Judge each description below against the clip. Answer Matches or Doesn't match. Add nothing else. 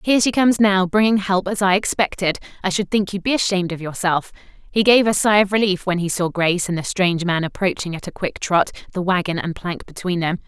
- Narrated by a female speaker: Matches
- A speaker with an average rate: Doesn't match